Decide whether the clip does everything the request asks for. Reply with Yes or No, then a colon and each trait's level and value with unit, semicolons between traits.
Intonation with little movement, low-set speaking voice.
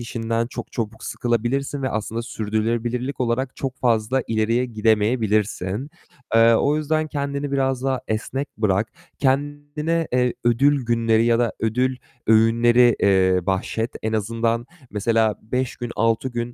No: average, 3.0 semitones; low, 120 Hz